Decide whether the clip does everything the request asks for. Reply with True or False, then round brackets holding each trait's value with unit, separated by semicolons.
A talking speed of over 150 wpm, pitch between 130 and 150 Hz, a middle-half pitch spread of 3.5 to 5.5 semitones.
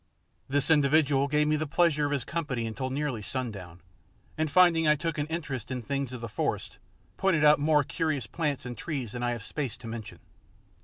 True (200 wpm; 140 Hz; 3.9 semitones)